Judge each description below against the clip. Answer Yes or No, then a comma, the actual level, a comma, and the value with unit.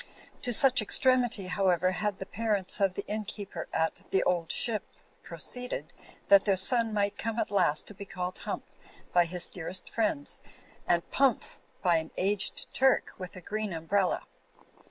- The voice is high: Yes, high, 200 Hz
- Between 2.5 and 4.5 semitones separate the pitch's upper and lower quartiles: Yes, average, 3.4 semitones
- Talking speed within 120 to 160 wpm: No, average, 170 wpm